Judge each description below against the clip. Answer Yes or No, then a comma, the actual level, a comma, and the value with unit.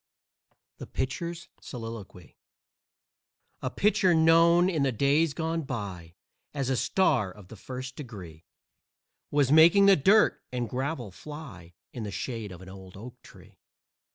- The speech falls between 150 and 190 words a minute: No, average, 140 wpm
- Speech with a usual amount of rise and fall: No, wide, 7.9 semitones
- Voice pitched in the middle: No, low, 130 Hz